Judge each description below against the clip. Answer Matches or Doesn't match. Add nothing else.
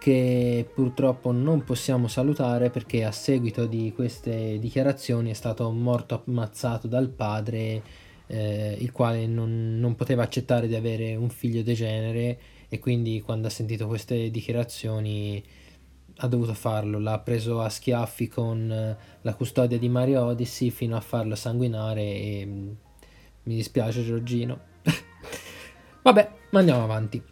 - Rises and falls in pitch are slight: Matches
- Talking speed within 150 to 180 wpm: Doesn't match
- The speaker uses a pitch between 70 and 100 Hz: Doesn't match